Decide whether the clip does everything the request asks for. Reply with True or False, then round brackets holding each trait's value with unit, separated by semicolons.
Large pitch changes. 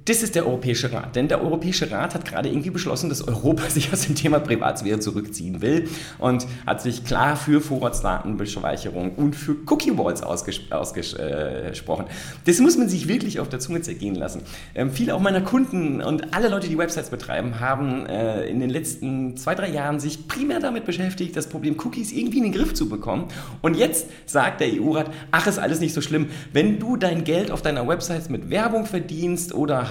True (6.0 semitones)